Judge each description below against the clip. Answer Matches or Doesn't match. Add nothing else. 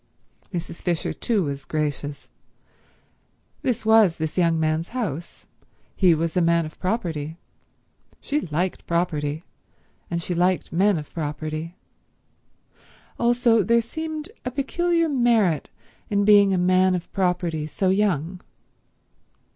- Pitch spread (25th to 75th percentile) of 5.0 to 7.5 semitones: Matches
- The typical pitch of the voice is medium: Matches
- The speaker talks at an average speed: Doesn't match